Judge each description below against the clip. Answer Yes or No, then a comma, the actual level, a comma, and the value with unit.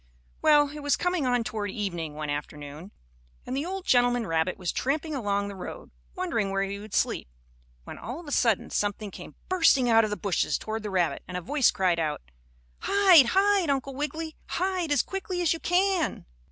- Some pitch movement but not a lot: No, wide, 8.5 semitones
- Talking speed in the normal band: Yes, average, 195 wpm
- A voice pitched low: No, high, 245 Hz